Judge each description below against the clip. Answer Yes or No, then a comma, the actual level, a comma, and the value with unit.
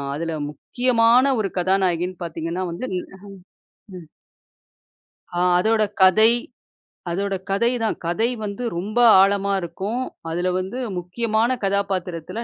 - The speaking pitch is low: No, high, 195 Hz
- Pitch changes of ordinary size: Yes, average, 4.1 semitones